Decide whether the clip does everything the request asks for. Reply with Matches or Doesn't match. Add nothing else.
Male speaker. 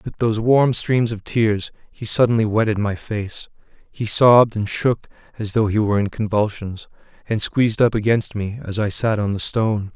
Matches